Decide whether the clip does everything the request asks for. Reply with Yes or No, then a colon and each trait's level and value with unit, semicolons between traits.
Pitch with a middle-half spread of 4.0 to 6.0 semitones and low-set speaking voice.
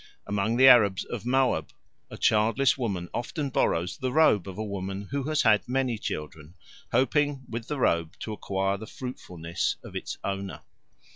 Yes: average, 5.2 semitones; low, 110 Hz